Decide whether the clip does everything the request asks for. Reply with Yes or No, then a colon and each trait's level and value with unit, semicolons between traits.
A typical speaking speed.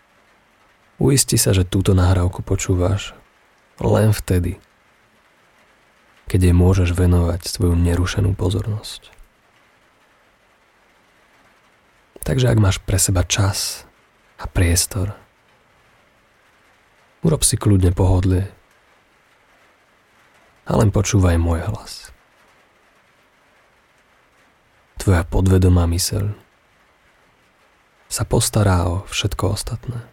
No: slow, 80 wpm